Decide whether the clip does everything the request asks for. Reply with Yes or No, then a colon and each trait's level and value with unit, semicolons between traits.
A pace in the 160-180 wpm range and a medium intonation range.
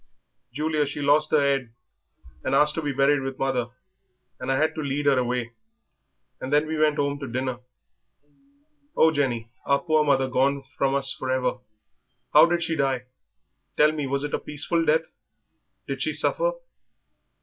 No: average, 170 wpm; narrow, 2.3 semitones